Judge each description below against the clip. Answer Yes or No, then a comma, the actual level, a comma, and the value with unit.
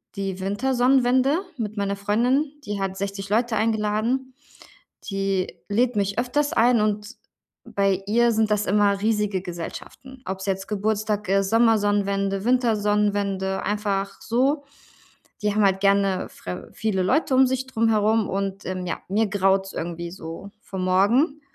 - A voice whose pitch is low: No, high, 205 Hz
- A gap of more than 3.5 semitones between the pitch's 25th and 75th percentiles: No, average, 2.8 semitones